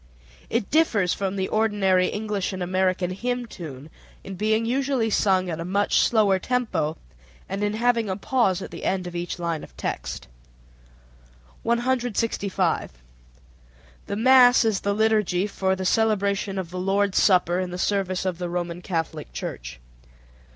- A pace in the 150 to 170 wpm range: Yes, average, 155 wpm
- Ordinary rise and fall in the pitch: Yes, average, 3.4 semitones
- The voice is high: Yes, high, 195 Hz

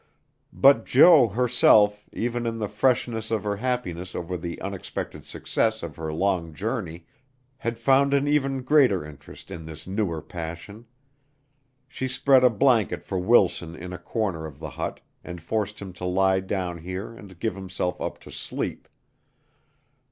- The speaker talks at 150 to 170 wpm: Yes, average, 160 wpm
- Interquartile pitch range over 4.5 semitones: Yes, average, 5.3 semitones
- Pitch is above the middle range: No, low, 100 Hz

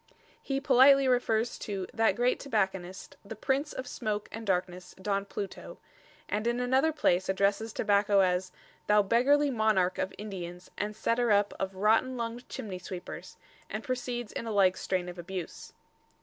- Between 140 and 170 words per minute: Yes, average, 160 wpm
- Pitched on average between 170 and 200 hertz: No, high, 210 Hz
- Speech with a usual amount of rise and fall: Yes, average, 4.2 semitones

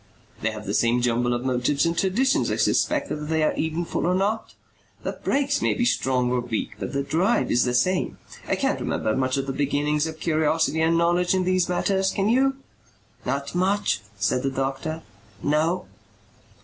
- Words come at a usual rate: Yes, average, 190 wpm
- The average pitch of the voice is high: No, medium, 155 Hz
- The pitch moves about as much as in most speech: No, wide, 6.0 semitones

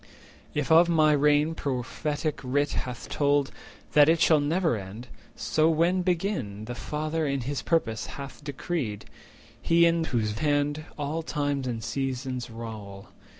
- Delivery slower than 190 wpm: Yes, average, 145 wpm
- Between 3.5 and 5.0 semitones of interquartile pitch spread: Yes, average, 4.3 semitones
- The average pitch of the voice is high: No, medium, 145 Hz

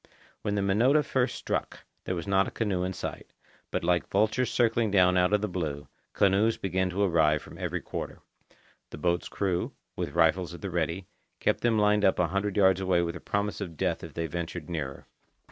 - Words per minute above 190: Yes, fast, 205 wpm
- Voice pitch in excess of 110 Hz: No, very low, 95 Hz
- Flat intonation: No, average, 3.2 semitones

